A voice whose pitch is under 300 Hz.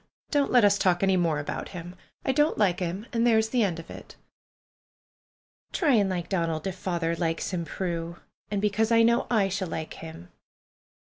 Yes: high, 190 Hz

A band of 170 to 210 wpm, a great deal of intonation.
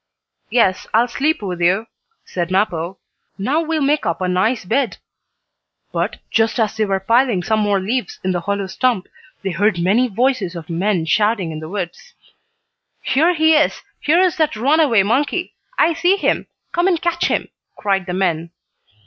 Yes: average, 175 wpm; wide, 6.8 semitones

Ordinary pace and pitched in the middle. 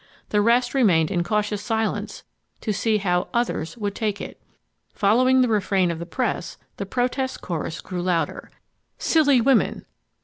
No: average, 150 wpm; high, 210 Hz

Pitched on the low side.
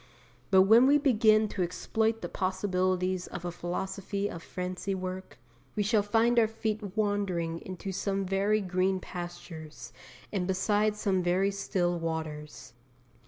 No: high, 190 Hz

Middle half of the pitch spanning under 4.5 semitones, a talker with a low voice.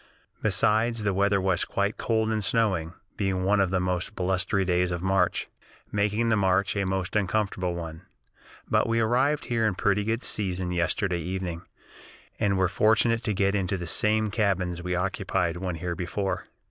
Yes: average, 2.8 semitones; very low, 95 Hz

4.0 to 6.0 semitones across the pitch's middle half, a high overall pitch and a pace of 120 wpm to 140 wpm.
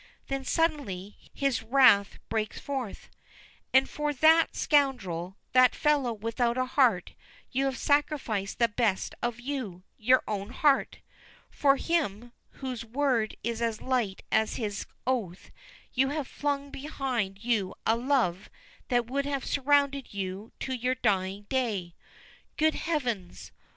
Yes: average, 4.7 semitones; high, 245 Hz; slow, 135 wpm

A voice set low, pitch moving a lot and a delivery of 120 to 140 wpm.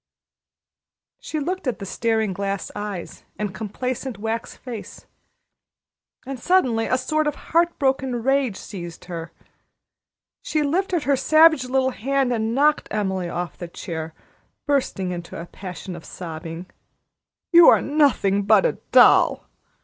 No: high, 230 Hz; wide, 6.7 semitones; slow, 135 wpm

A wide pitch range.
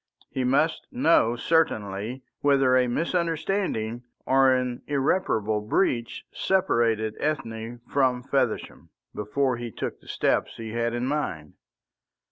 No: average, 3.9 semitones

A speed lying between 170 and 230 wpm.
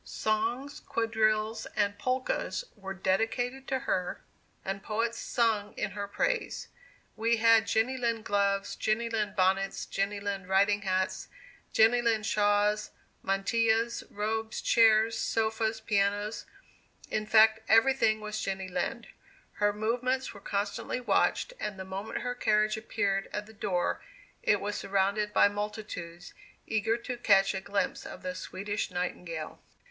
No: average, 140 wpm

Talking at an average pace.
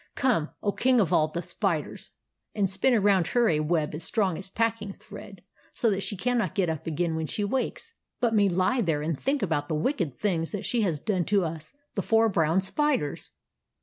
No: fast, 215 wpm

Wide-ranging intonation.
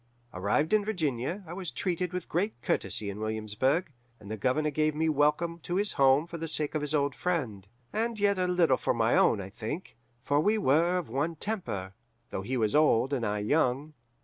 Yes: wide, 6.5 semitones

